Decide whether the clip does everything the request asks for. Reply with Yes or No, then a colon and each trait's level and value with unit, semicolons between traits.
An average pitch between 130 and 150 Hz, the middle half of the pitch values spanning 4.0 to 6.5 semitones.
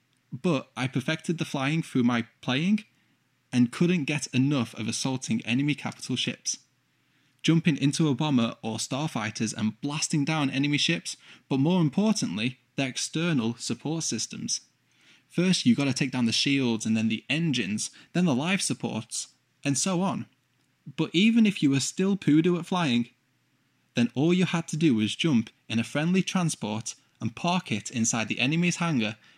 Yes: medium, 140 Hz; average, 5.2 semitones